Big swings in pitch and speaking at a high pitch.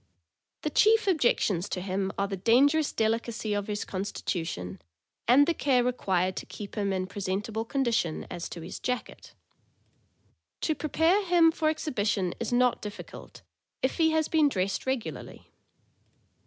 Yes: wide, 6.8 semitones; high, 225 Hz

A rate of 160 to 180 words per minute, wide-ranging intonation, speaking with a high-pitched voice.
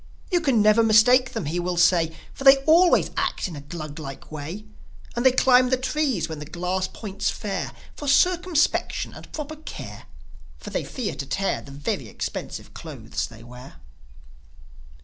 Yes: average, 170 wpm; wide, 8.8 semitones; high, 210 Hz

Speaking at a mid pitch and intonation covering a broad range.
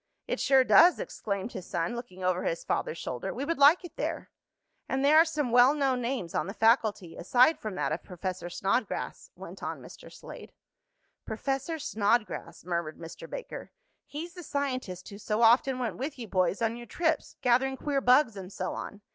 No: high, 240 Hz; wide, 6.4 semitones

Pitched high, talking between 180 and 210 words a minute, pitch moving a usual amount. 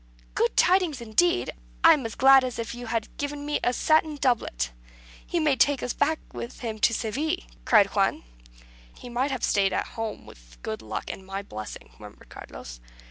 No: high, 240 Hz; average, 190 wpm; wide, 6.3 semitones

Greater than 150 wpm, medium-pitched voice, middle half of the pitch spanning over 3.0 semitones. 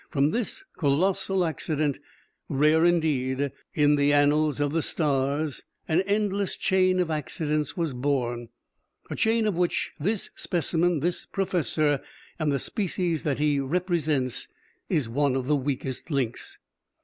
No: slow, 135 wpm; medium, 150 Hz; average, 4.0 semitones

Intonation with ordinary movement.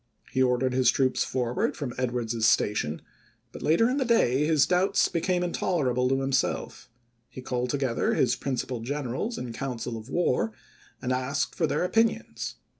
Yes: average, 4.0 semitones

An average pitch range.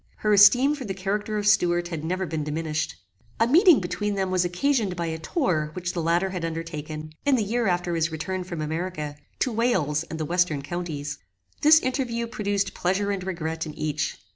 Yes: average, 4.5 semitones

